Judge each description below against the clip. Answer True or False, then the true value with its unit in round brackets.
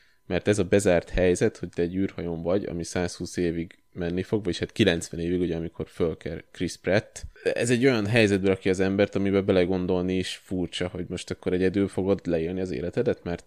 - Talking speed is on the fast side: True (190 wpm)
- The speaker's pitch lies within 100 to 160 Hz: False (90 Hz)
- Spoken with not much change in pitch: True (2.2 semitones)